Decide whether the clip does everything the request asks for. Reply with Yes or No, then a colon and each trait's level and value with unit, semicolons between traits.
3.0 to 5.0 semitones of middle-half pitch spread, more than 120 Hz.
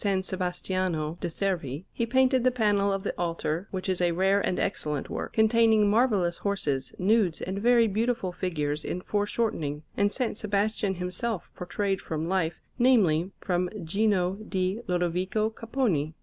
Yes: average, 3.7 semitones; high, 190 Hz